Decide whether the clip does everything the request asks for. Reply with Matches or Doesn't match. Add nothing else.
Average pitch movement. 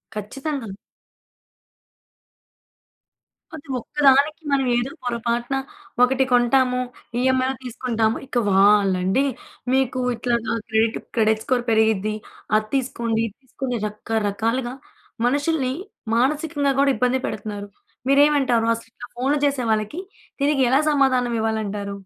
Matches